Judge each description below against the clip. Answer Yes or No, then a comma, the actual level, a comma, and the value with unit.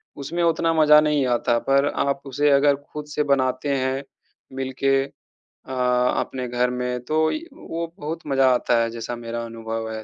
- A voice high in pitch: No, low, 135 Hz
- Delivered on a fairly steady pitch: No, average, 3.3 semitones